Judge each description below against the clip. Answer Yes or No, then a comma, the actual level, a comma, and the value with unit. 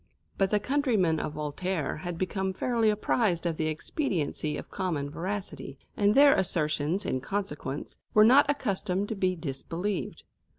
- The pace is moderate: Yes, average, 145 wpm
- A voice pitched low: No, medium, 185 Hz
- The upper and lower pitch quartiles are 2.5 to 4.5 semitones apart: No, average, 5.0 semitones